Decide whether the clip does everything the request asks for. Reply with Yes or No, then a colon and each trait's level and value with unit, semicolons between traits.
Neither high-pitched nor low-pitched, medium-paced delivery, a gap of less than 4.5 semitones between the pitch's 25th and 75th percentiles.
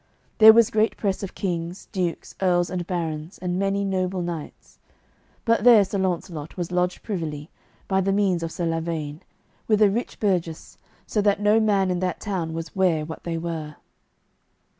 Yes: medium, 180 Hz; average, 175 wpm; average, 3.1 semitones